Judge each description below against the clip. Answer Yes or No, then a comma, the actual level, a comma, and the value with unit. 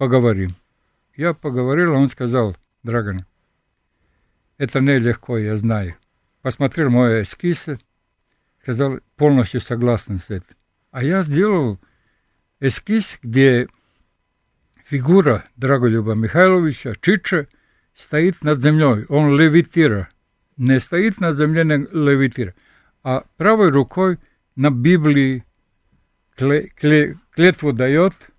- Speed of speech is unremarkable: No, slow, 100 wpm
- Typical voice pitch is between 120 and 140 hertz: Yes, low, 135 Hz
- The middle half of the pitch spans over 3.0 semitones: Yes, wide, 5.4 semitones